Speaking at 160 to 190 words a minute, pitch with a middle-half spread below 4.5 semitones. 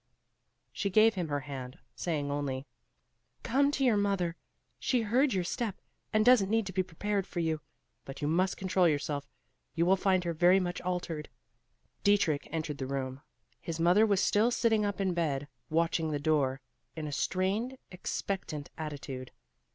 No: average, 165 wpm; average, 5.3 semitones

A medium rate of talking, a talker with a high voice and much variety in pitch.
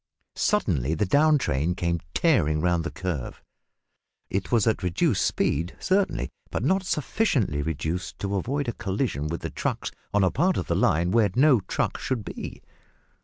No: average, 170 wpm; very low, 95 Hz; wide, 7.9 semitones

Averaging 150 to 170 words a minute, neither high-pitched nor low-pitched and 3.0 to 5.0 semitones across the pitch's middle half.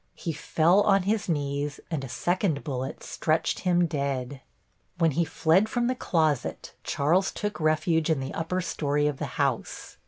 Yes: average, 165 wpm; medium, 160 Hz; average, 4.0 semitones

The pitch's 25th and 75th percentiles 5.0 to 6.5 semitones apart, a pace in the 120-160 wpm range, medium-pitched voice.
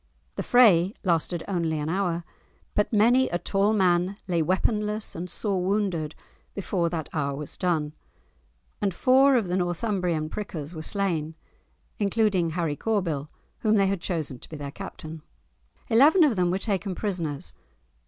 No: average, 4.3 semitones; average, 155 wpm; medium, 180 Hz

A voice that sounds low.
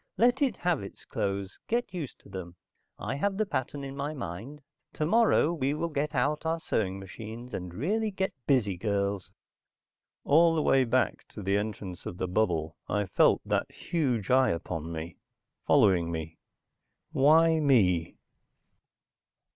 Yes: low, 125 Hz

